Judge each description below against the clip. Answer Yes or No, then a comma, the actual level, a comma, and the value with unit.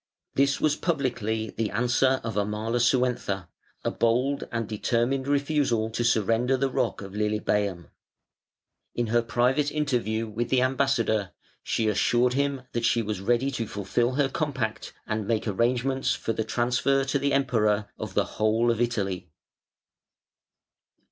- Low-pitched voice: Yes, low, 120 Hz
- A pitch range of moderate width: Yes, average, 3.5 semitones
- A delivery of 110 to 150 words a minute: Yes, average, 145 wpm